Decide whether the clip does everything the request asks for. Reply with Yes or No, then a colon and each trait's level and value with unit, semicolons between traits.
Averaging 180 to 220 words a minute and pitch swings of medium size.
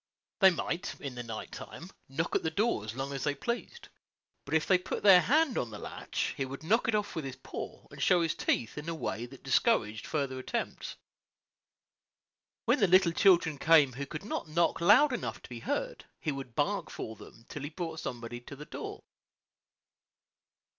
No: average, 200 wpm; wide, 5.9 semitones